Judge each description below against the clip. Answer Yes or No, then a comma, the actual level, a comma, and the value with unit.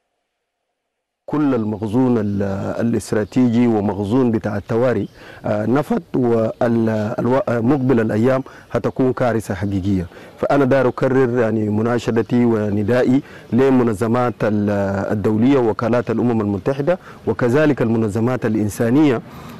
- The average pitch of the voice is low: Yes, low, 120 Hz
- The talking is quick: No, average, 80 wpm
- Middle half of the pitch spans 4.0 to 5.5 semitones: No, average, 3.3 semitones